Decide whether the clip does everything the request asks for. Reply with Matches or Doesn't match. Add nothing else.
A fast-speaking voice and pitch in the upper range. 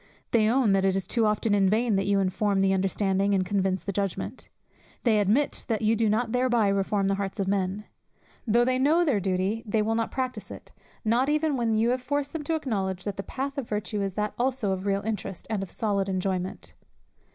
Matches